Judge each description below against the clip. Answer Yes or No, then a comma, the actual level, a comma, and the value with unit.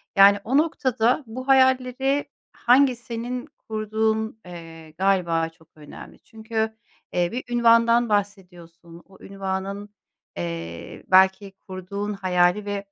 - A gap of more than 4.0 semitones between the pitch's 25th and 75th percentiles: Yes, average, 4.5 semitones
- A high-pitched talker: Yes, high, 205 Hz